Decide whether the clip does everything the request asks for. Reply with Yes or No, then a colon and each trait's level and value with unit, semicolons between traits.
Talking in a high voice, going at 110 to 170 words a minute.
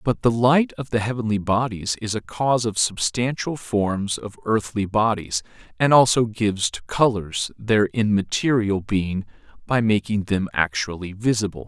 No: low, 110 Hz; average, 150 wpm